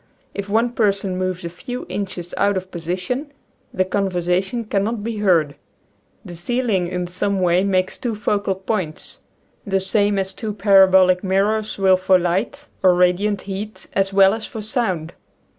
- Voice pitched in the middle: No, high, 195 Hz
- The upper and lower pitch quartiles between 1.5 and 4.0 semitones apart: Yes, narrow, 2.4 semitones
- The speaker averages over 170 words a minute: No, average, 160 wpm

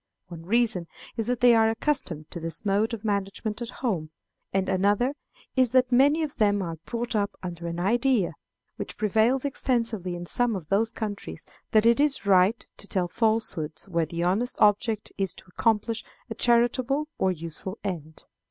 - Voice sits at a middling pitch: No, high, 210 Hz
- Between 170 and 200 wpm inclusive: Yes, average, 175 wpm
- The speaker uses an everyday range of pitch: Yes, average, 4.6 semitones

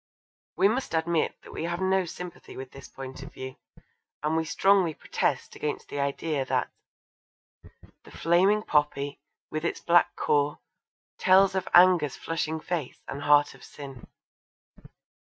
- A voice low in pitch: No, medium, 160 Hz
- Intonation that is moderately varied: Yes, average, 3.8 semitones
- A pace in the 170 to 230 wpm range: No, average, 145 wpm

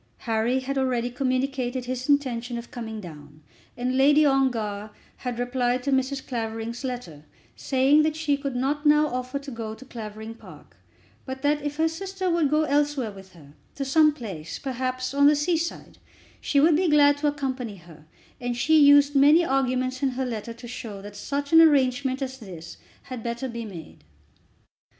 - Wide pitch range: No, average, 3.6 semitones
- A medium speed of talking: Yes, average, 180 wpm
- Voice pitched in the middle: No, very high, 260 Hz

